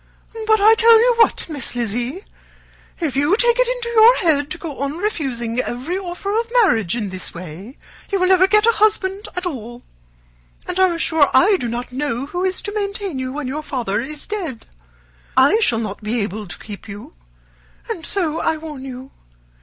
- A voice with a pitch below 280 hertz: No, very high, 305 Hz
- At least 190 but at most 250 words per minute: Yes, average, 195 wpm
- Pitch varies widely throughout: Yes, wide, 8.5 semitones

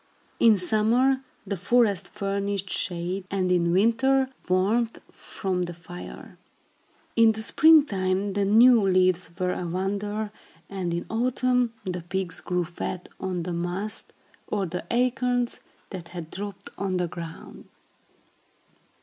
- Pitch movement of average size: Yes, average, 3.9 semitones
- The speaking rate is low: Yes, slow, 130 wpm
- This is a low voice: No, high, 195 Hz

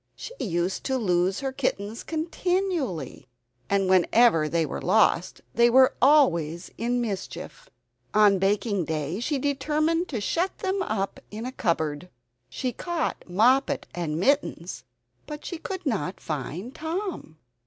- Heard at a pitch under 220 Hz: No, high, 225 Hz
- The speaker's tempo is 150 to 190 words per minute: No, slow, 135 wpm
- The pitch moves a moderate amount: No, wide, 8.6 semitones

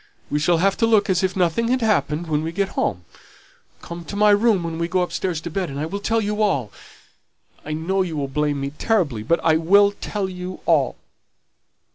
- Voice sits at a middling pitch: Yes, medium, 175 Hz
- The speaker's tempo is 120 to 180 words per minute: No, fast, 205 wpm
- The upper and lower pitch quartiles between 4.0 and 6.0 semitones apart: Yes, average, 4.4 semitones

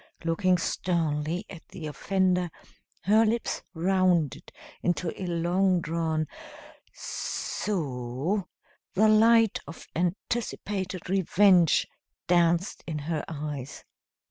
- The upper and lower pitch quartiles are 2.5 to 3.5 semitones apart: Yes, average, 3.0 semitones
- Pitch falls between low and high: Yes, medium, 175 Hz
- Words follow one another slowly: Yes, slow, 95 wpm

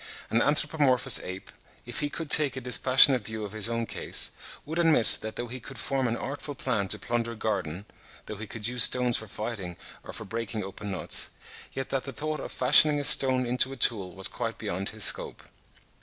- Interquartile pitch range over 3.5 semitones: Yes, average, 3.9 semitones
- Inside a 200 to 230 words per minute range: Yes, fast, 205 wpm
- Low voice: Yes, low, 120 Hz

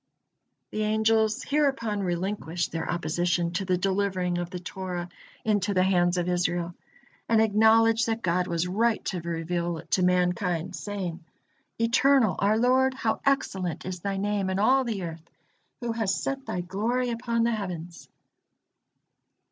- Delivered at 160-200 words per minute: No, average, 150 wpm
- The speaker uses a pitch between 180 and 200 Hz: Yes, high, 190 Hz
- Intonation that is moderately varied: Yes, average, 4.2 semitones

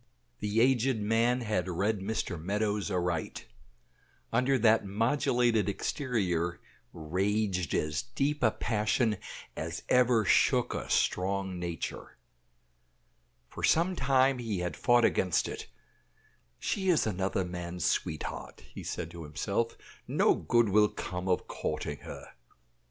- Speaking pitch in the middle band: No, low, 105 Hz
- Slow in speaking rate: Yes, slow, 125 wpm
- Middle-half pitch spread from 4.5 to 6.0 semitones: Yes, average, 4.9 semitones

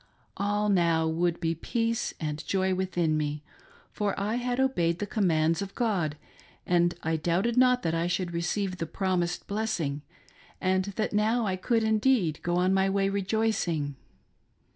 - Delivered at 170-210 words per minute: No, average, 160 wpm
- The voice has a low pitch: No, medium, 185 Hz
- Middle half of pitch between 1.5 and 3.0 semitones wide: No, average, 4.0 semitones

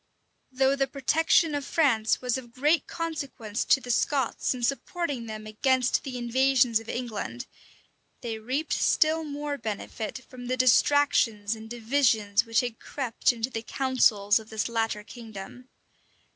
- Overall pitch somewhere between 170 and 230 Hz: No, very high, 250 Hz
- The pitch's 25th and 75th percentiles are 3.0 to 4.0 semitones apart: Yes, average, 3.5 semitones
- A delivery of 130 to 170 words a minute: Yes, average, 145 wpm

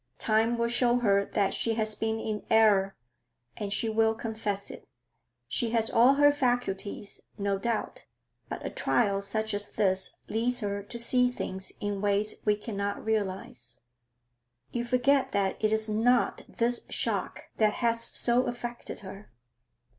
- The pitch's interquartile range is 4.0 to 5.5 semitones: No, average, 2.8 semitones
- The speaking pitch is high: Yes, high, 220 Hz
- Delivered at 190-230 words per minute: No, average, 155 wpm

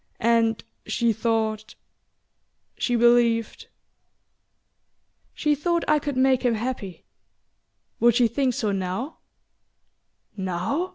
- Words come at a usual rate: No, slow, 105 wpm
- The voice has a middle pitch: No, high, 235 Hz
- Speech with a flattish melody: No, average, 3.1 semitones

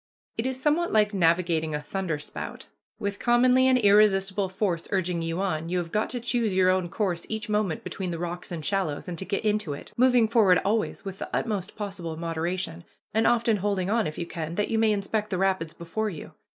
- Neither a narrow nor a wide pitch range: Yes, average, 4.1 semitones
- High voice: Yes, high, 195 Hz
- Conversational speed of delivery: No, fast, 215 wpm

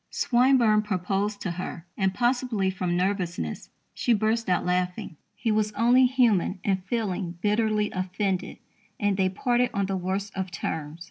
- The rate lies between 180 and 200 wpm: No, average, 150 wpm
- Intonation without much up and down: No, average, 3.2 semitones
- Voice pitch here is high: Yes, high, 200 Hz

